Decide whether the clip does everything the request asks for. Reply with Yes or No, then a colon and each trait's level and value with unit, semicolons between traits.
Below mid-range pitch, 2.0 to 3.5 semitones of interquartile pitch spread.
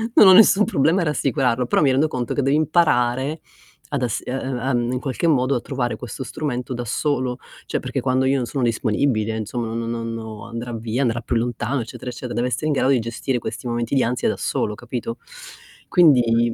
Yes: low, 125 Hz; average, 2.7 semitones